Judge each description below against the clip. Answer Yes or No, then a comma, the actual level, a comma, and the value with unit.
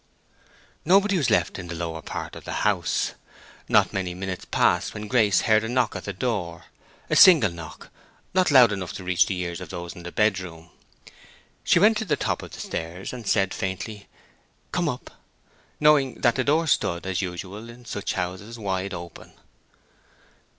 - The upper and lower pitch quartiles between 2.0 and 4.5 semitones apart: No, wide, 5.5 semitones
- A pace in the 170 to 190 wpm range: Yes, average, 180 wpm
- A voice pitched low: Yes, low, 100 Hz